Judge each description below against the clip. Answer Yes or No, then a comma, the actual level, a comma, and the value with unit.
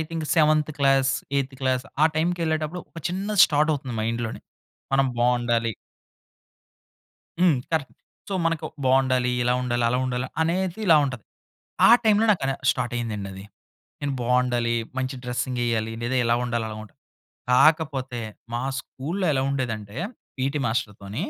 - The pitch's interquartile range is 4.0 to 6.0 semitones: Yes, average, 4.4 semitones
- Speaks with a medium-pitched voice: No, low, 130 Hz